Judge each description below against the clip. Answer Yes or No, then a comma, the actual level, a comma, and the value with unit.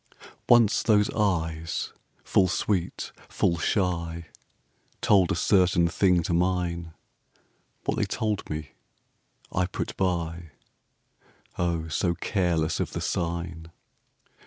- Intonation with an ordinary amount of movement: No, narrow, 2.1 semitones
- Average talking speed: No, slow, 110 wpm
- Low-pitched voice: Yes, very low, 85 Hz